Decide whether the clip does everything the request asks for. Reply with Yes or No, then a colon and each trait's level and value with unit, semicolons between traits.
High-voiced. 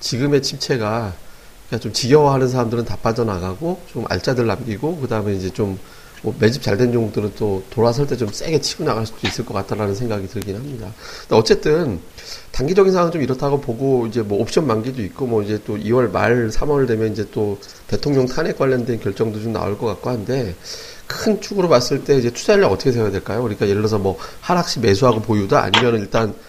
No: low, 115 Hz